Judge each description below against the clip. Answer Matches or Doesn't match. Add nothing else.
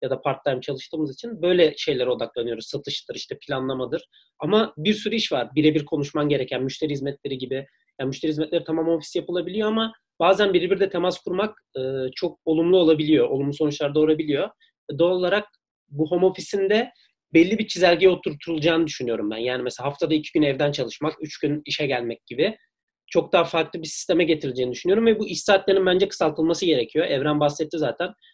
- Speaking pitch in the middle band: Matches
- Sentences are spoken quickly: Matches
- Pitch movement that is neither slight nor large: Matches